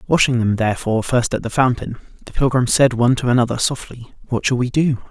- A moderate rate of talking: No, fast, 210 wpm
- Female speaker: No, male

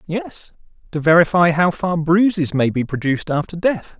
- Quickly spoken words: No, average, 165 wpm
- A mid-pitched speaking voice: Yes, medium, 165 Hz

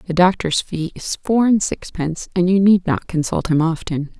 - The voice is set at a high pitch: No, medium, 175 Hz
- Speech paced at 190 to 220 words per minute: Yes, average, 200 wpm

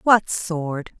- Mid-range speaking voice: Yes, medium, 175 Hz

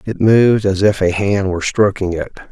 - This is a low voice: Yes, low, 100 Hz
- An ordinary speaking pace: No, fast, 215 wpm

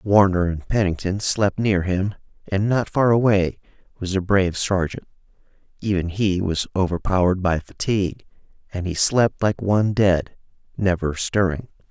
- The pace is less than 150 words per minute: Yes, average, 140 wpm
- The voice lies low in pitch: Yes, very low, 95 Hz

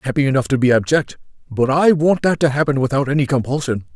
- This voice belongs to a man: Yes, male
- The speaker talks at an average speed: No, fast, 230 wpm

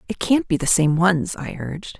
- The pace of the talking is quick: Yes, fast, 240 wpm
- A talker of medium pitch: Yes, medium, 170 Hz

